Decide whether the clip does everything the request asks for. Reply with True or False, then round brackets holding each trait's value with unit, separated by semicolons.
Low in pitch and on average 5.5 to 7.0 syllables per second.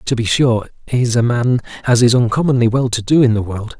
True (120 Hz; 5.6 syllables/s)